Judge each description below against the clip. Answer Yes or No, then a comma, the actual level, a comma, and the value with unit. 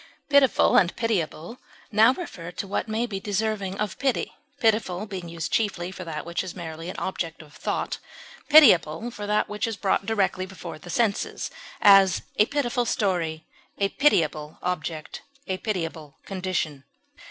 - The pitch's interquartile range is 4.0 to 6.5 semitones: Yes, average, 4.5 semitones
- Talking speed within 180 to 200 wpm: No, average, 155 wpm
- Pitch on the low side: No, high, 190 Hz